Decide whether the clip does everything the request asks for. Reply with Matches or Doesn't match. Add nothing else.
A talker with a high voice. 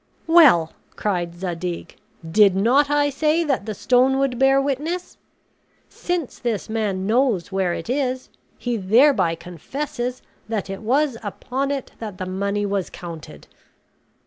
Matches